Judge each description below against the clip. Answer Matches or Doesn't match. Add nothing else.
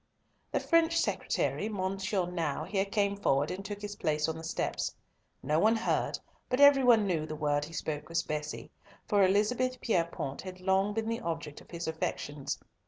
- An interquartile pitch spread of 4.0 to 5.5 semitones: Matches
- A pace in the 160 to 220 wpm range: Matches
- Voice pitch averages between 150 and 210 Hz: Matches